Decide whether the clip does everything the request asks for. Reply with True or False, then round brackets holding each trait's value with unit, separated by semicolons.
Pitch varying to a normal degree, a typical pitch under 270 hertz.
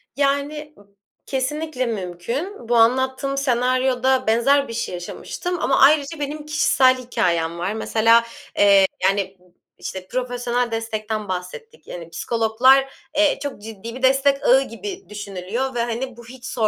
True (3.9 semitones; 245 Hz)